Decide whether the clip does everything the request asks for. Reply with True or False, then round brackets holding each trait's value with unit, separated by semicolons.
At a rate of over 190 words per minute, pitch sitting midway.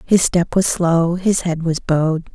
True (205 wpm; 170 Hz)